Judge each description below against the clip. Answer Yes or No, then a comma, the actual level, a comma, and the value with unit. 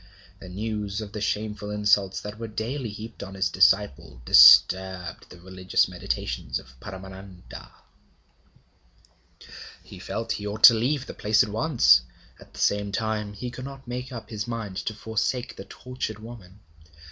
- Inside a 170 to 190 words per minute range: No, average, 160 wpm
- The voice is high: No, low, 105 Hz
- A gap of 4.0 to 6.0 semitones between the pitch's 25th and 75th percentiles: No, average, 2.8 semitones